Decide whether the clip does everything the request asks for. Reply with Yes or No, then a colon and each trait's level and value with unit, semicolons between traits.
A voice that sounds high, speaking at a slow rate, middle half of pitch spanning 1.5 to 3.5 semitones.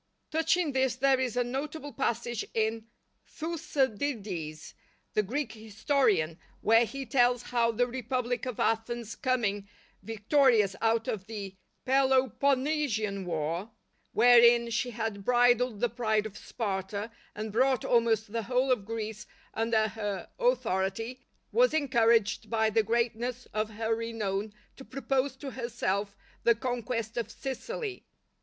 Yes: high, 230 Hz; slow, 130 wpm; average, 3.1 semitones